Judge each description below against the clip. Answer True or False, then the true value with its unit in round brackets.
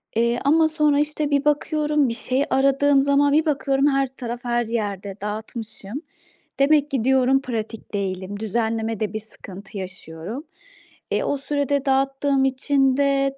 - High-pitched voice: True (265 Hz)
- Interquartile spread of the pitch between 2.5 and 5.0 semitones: True (4.3 semitones)